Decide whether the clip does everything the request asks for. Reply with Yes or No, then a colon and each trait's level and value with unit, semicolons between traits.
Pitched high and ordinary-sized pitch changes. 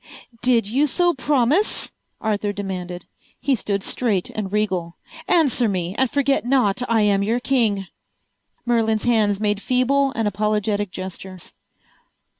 Yes: high, 215 Hz; average, 4.1 semitones